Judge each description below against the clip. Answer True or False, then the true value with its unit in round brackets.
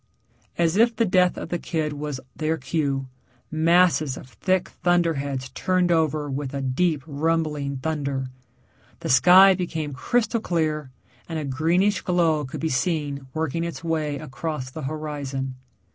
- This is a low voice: False (155 Hz)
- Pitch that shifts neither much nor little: True (3.6 semitones)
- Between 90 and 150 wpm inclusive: True (145 wpm)